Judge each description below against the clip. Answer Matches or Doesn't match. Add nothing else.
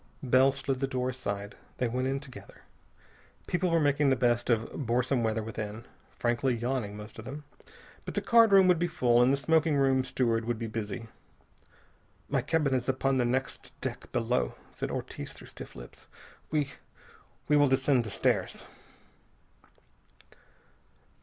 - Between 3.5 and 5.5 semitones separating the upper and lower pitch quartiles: Doesn't match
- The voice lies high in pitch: Doesn't match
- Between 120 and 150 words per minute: Doesn't match